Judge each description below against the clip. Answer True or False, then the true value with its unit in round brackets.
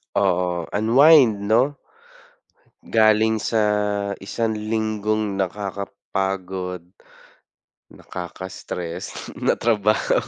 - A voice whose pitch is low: True (105 Hz)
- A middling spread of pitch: False (2.3 semitones)